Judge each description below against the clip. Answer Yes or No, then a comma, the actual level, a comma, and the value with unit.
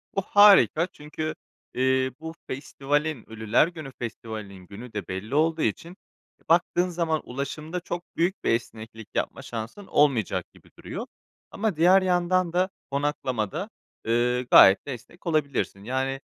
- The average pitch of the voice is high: No, medium, 145 Hz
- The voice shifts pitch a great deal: Yes, wide, 6.7 semitones